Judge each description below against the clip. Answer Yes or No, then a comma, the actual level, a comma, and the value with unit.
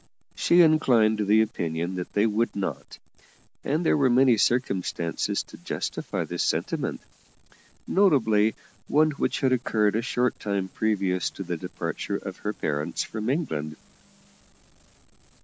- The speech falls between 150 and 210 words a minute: No, slow, 135 wpm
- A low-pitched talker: Yes, low, 110 Hz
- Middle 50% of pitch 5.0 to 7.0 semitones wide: Yes, average, 5.3 semitones